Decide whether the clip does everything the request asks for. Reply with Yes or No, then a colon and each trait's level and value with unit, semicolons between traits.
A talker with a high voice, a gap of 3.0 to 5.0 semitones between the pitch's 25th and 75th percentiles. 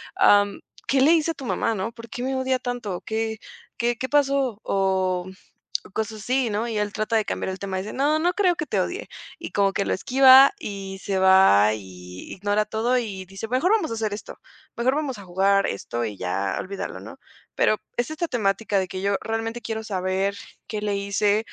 Yes: high, 215 Hz; average, 4.6 semitones